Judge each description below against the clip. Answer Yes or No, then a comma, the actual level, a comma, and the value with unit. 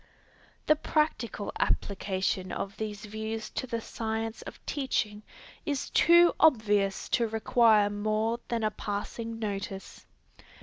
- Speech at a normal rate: No, slow, 120 wpm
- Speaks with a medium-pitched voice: No, high, 220 Hz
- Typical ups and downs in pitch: No, narrow, 2.2 semitones